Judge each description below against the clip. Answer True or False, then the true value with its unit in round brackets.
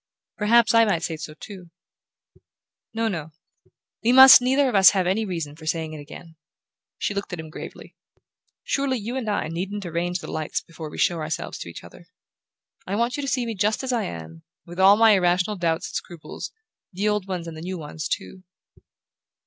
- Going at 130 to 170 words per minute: False (200 wpm)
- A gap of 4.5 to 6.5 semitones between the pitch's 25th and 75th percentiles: True (5.2 semitones)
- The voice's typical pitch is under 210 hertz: True (185 Hz)